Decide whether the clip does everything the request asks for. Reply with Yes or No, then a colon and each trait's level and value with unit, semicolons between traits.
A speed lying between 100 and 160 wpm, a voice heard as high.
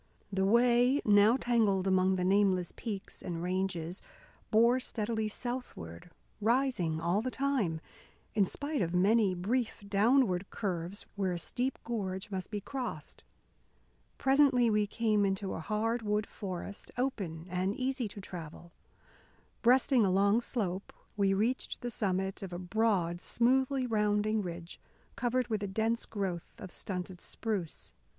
Yes: average, 140 wpm; high, 205 Hz